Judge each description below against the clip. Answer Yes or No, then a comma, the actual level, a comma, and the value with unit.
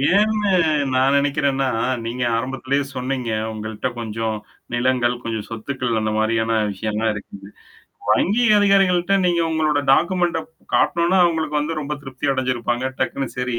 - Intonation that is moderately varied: No, wide, 5.7 semitones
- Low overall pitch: Yes, low, 130 Hz